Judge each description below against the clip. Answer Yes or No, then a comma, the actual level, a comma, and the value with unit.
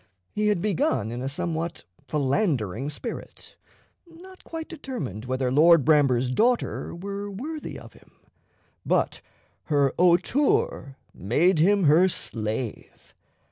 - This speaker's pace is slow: Yes, slow, 115 wpm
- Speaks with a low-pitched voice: No, medium, 165 Hz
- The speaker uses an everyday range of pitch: No, wide, 7.7 semitones